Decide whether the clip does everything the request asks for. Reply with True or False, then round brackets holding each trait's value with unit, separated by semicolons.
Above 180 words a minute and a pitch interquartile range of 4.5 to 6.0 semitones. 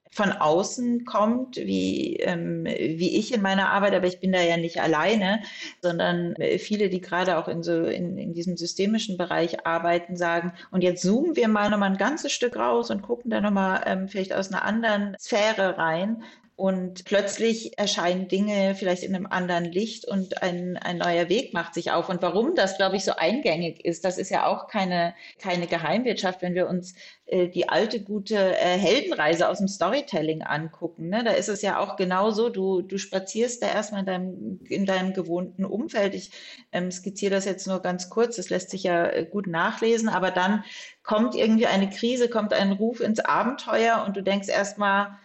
False (190 wpm; 2.8 semitones)